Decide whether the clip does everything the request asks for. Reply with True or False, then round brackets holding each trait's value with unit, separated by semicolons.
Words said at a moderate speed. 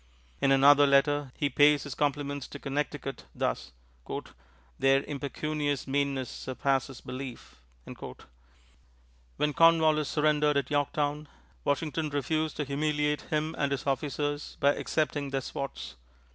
False (115 wpm)